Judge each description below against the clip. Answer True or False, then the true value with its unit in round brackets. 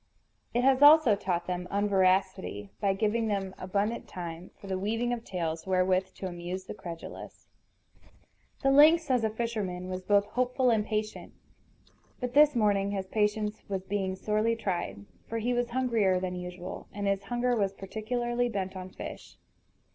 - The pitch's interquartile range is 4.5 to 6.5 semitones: False (4.0 semitones)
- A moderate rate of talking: True (160 wpm)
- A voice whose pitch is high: True (205 Hz)